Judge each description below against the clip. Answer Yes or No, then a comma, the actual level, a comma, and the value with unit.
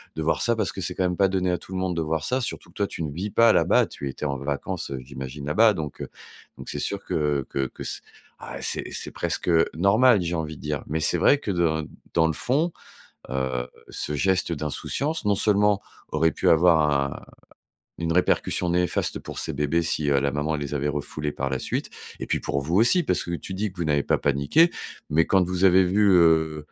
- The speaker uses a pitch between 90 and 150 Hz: No, very low, 80 Hz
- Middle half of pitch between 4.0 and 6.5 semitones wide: Yes, average, 4.6 semitones